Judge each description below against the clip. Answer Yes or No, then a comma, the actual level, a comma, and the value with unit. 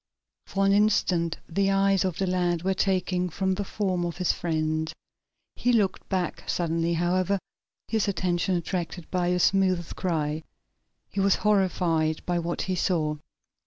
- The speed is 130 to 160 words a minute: Yes, average, 155 wpm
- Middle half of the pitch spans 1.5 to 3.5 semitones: Yes, narrow, 2.4 semitones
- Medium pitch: Yes, medium, 180 Hz